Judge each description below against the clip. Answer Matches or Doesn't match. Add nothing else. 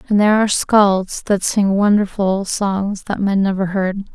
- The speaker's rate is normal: Matches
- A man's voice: Doesn't match